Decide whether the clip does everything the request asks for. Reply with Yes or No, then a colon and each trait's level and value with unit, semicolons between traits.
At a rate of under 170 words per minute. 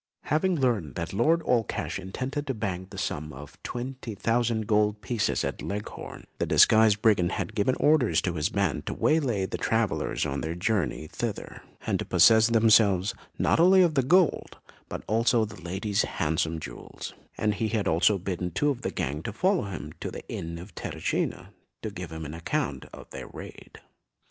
No: average, 185 wpm